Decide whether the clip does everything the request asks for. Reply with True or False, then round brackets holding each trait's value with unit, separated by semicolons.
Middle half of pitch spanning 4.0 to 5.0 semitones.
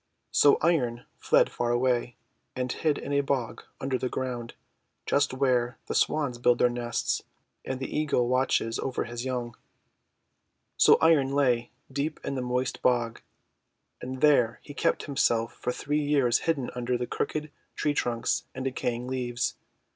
False (2.6 semitones)